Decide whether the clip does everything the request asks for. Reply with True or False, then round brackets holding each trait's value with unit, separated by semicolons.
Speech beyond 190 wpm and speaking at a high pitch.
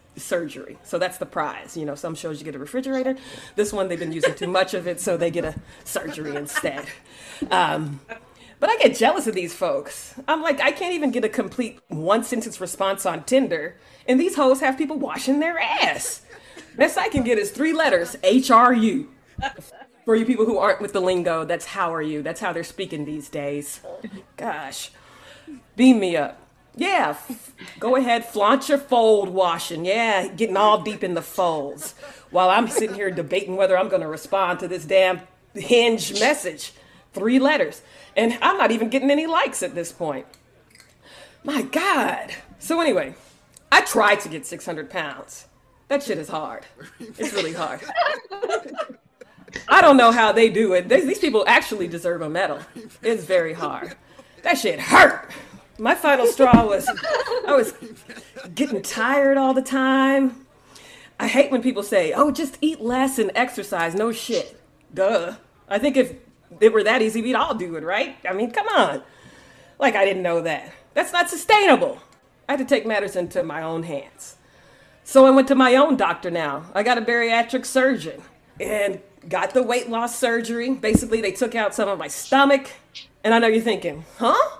False (185 wpm; 225 Hz)